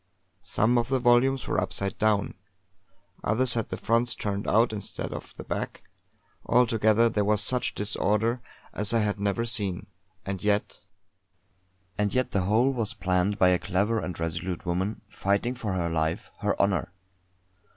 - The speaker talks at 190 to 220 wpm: No, average, 160 wpm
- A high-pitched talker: No, low, 105 Hz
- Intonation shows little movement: No, average, 3.2 semitones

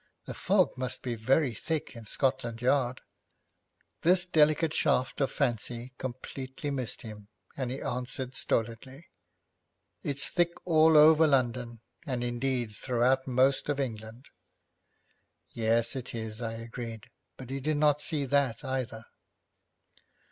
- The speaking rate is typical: No, slow, 130 wpm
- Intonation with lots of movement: No, average, 3.2 semitones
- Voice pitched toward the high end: No, low, 130 Hz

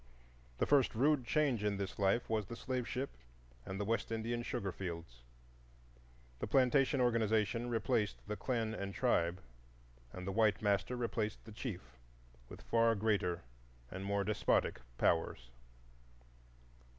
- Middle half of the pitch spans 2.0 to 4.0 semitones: Yes, average, 3.5 semitones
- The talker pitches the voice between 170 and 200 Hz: No, low, 110 Hz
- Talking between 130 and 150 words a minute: Yes, average, 140 wpm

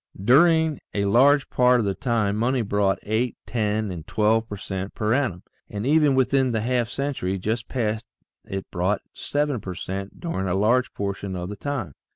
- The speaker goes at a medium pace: Yes, average, 185 wpm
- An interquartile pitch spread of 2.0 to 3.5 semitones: No, average, 4.4 semitones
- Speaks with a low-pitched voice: Yes, low, 110 Hz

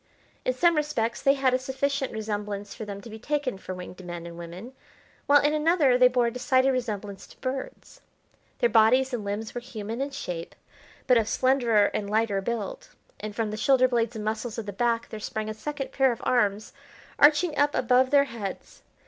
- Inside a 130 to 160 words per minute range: No, average, 200 wpm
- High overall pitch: Yes, high, 235 Hz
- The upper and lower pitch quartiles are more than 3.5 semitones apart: Yes, average, 4.0 semitones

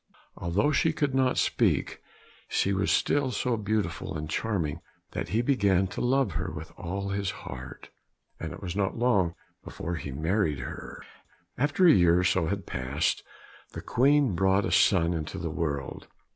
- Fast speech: No, average, 170 wpm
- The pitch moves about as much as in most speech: No, wide, 6.1 semitones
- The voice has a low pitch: Yes, very low, 95 Hz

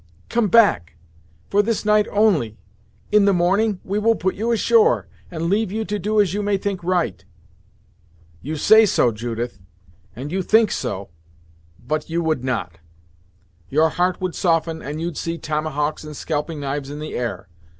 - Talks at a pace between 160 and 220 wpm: Yes, average, 170 wpm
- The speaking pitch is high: No, medium, 170 Hz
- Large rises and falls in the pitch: Yes, wide, 5.8 semitones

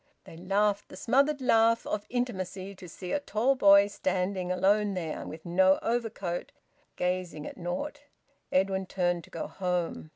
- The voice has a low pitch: No, high, 190 Hz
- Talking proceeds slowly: No, average, 155 wpm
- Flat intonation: No, average, 3.0 semitones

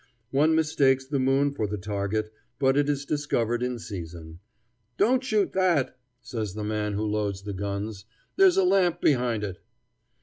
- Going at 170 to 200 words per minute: No, average, 160 wpm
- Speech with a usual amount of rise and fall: No, wide, 5.8 semitones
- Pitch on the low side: Yes, low, 120 Hz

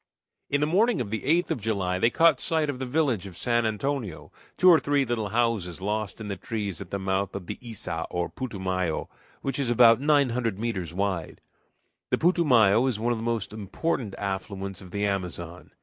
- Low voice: Yes, low, 110 Hz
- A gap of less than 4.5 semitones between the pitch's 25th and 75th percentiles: No, average, 5.2 semitones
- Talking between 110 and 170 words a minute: No, average, 200 wpm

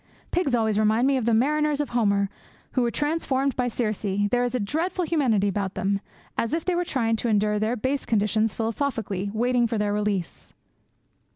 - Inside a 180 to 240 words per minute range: Yes, average, 190 wpm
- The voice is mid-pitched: No, high, 230 Hz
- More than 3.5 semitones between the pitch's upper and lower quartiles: Yes, average, 4.4 semitones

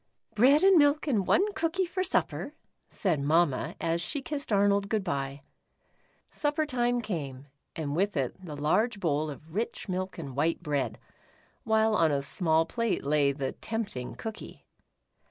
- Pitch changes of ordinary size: No, wide, 8.1 semitones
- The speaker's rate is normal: Yes, average, 160 wpm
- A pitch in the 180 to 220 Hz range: Yes, medium, 185 Hz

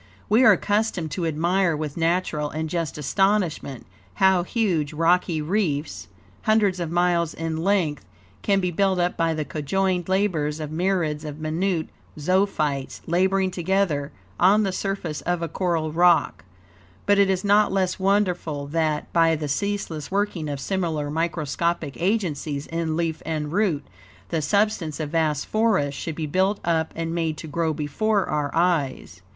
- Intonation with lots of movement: No, average, 3.8 semitones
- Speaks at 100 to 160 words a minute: Yes, average, 155 wpm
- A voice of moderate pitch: Yes, medium, 170 Hz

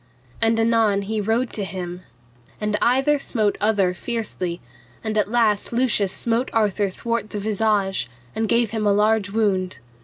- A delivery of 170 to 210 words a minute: No, average, 155 wpm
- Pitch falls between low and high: No, high, 215 Hz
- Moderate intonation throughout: No, narrow, 2.3 semitones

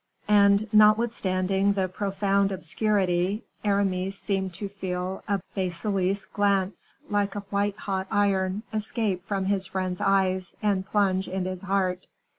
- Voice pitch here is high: Yes, high, 195 Hz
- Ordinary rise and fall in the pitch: No, narrow, 1.5 semitones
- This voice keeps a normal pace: No, slow, 130 wpm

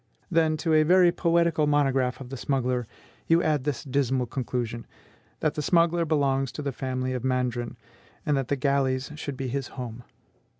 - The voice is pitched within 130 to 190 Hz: Yes, low, 135 Hz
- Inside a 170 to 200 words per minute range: Yes, average, 175 wpm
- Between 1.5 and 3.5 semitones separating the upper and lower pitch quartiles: Yes, average, 3.2 semitones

